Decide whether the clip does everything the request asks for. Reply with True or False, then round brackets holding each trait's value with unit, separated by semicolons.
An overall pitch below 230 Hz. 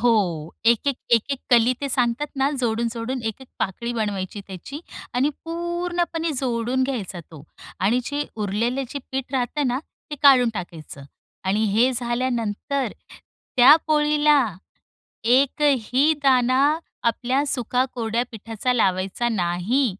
False (245 Hz)